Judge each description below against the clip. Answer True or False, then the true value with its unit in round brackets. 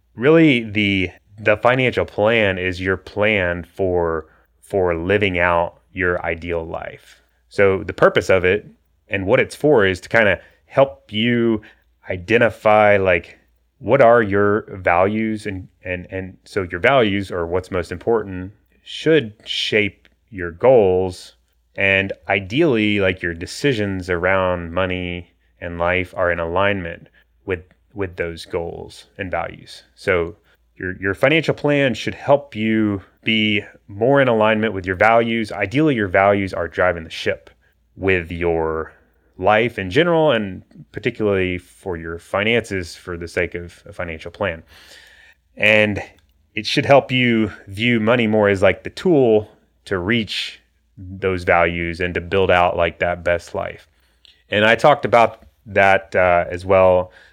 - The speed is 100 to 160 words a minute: True (145 wpm)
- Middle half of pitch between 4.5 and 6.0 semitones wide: False (3.7 semitones)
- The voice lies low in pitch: True (95 Hz)